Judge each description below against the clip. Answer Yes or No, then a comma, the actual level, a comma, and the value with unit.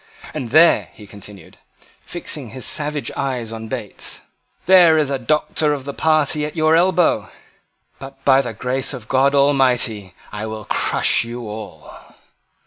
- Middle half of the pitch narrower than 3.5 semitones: No, average, 4.9 semitones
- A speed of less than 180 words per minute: Yes, average, 150 wpm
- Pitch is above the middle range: No, low, 135 Hz